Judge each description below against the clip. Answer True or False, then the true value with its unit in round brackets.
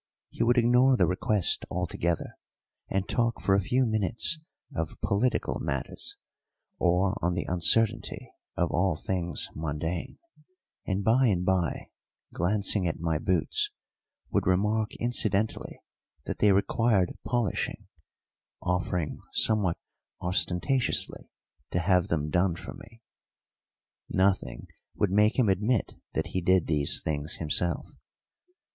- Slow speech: True (120 wpm)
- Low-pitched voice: True (95 Hz)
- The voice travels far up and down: False (4.0 semitones)